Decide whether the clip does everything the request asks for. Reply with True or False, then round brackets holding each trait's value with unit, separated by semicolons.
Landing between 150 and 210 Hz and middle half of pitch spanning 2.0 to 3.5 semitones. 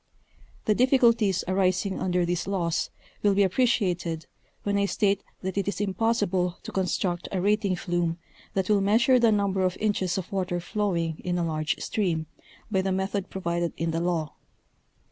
True (190 Hz; 2.6 semitones)